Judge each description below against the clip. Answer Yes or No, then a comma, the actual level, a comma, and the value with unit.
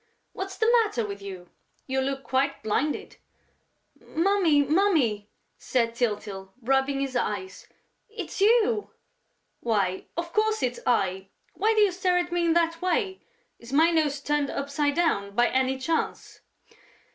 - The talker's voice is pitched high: Yes, very high, 280 Hz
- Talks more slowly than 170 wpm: Yes, average, 145 wpm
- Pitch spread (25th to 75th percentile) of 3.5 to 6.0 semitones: No, wide, 7.1 semitones